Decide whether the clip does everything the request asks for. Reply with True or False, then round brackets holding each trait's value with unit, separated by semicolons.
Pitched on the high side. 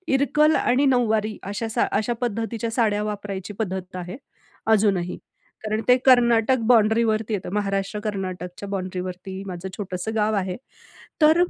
True (210 Hz)